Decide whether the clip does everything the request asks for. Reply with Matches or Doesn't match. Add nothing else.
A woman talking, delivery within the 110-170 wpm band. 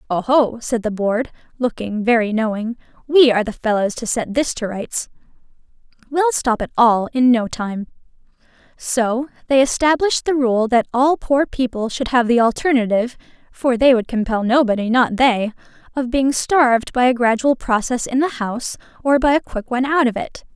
Doesn't match